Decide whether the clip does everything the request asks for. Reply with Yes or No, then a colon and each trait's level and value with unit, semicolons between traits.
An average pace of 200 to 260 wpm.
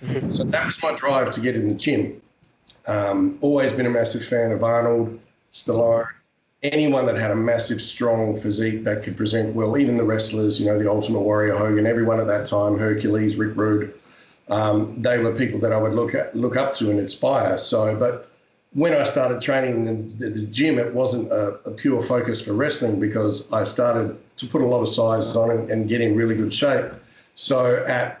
Yes: fast, 205 wpm